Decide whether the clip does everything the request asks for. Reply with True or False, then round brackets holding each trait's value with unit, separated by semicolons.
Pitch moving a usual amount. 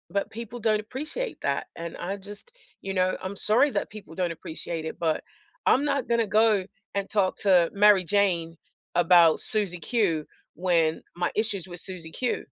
True (3.9 semitones)